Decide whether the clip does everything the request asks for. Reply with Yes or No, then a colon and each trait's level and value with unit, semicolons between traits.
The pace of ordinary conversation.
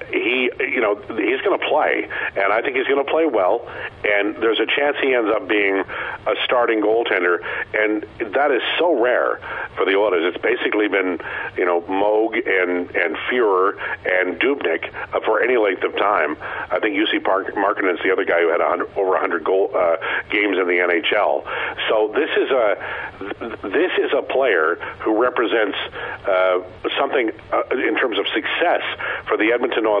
Yes: average, 185 wpm